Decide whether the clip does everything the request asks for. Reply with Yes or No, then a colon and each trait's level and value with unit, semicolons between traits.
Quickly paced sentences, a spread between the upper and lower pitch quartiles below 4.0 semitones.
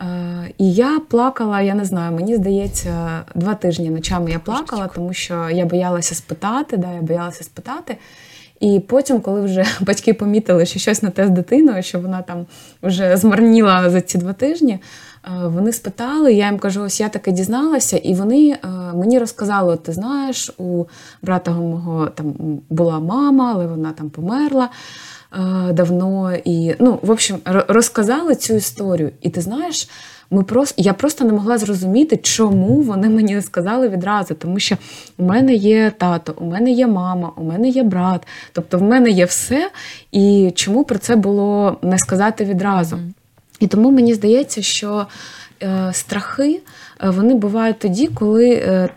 No: fast, 160 wpm; average, 4.5 semitones